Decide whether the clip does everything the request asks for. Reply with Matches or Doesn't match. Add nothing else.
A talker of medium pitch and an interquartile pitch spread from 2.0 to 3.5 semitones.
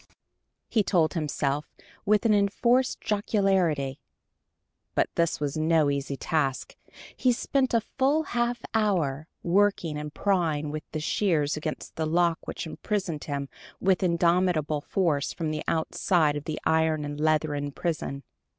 Doesn't match